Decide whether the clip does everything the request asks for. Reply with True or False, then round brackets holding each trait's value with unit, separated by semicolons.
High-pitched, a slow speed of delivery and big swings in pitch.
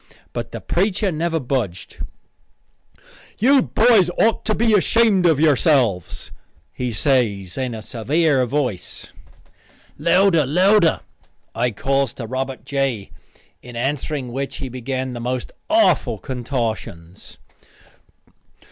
False (135 Hz; 110 wpm; 6.0 semitones)